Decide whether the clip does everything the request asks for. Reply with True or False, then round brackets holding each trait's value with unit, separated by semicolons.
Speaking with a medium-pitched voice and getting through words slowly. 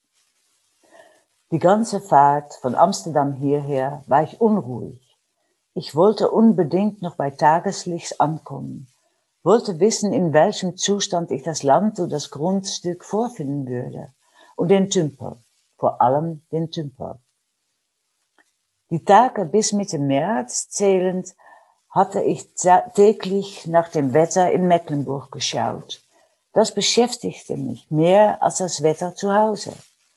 True (175 Hz; 120 wpm)